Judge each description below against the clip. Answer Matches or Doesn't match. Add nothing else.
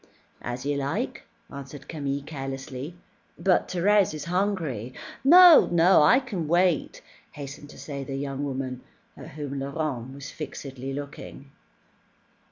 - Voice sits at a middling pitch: Matches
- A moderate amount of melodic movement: Matches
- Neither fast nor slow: Doesn't match